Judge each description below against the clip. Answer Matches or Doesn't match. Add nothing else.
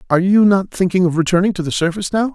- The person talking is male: Matches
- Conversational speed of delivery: Doesn't match